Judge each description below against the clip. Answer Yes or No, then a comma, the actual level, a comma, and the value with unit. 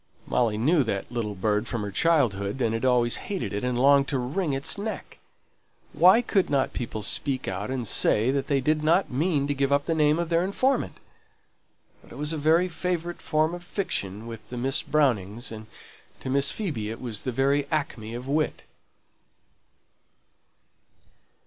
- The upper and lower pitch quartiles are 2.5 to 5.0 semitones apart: No, wide, 5.5 semitones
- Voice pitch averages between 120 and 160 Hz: Yes, low, 135 Hz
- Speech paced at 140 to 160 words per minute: No, average, 180 wpm